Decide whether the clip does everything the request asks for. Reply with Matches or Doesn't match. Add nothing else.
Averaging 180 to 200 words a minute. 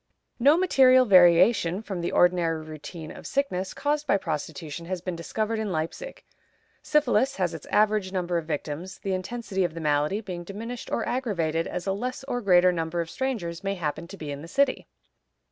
Matches